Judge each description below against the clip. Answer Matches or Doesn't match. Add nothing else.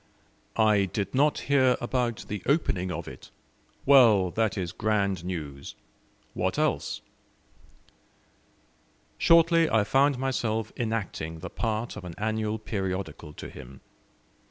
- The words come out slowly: Matches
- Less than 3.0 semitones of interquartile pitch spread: Doesn't match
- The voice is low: Matches